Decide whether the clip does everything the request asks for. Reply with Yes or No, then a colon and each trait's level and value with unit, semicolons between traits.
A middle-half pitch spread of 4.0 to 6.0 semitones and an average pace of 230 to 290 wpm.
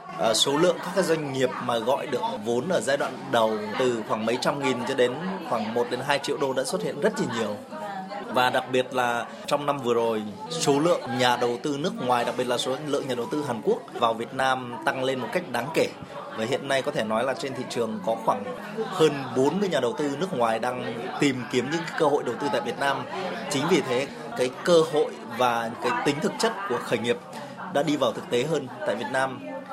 No: average, 3.5 semitones; average, 240 wpm